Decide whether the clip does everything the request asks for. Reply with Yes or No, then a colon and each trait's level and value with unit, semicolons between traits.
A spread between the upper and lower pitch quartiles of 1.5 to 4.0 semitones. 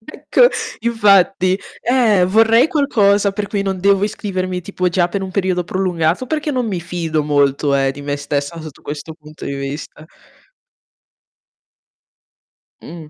No: average, 4.8 semitones